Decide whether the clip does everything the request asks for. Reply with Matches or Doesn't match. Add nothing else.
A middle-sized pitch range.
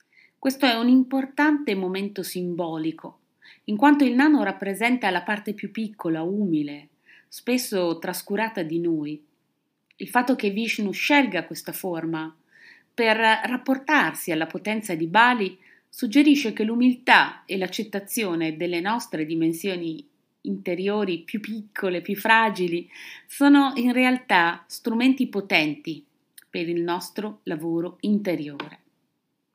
Doesn't match